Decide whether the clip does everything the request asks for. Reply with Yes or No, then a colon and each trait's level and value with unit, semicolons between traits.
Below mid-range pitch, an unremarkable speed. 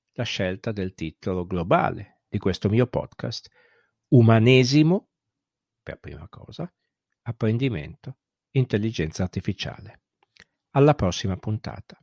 No: low, 110 Hz; slow, 95 wpm